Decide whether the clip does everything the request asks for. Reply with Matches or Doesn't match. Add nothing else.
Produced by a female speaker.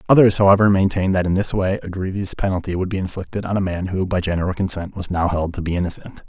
Doesn't match